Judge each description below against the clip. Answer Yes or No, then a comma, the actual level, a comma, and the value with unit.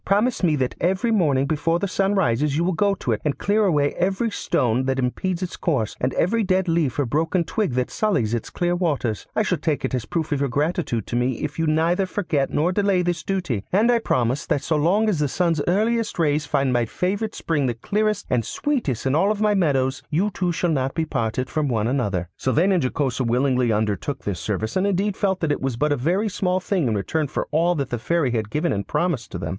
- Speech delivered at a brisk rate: Yes, fast, 240 wpm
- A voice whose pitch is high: No, medium, 155 Hz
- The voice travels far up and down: Yes, wide, 6.4 semitones